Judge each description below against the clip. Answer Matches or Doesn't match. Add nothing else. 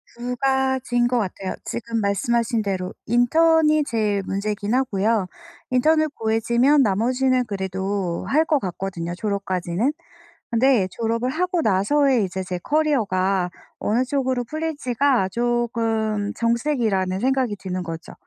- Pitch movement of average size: Matches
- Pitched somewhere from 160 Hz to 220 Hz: Doesn't match